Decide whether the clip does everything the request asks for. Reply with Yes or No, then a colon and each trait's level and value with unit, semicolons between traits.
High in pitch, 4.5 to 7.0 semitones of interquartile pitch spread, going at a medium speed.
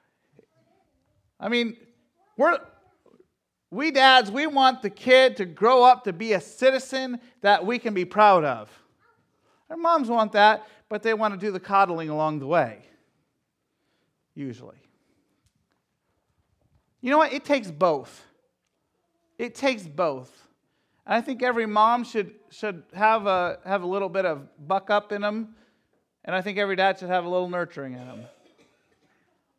Yes: high, 210 Hz; average, 5.0 semitones; average, 155 wpm